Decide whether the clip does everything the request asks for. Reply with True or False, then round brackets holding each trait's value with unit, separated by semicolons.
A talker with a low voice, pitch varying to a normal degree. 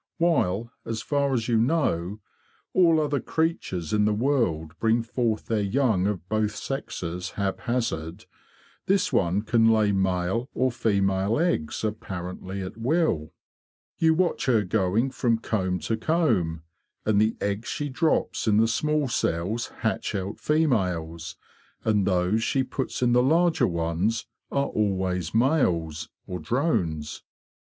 False (110 Hz; 6.0 semitones)